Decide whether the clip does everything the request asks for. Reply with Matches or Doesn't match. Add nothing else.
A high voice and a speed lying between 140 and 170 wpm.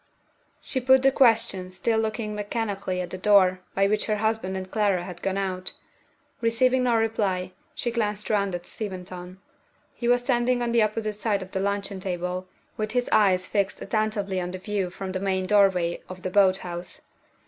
Doesn't match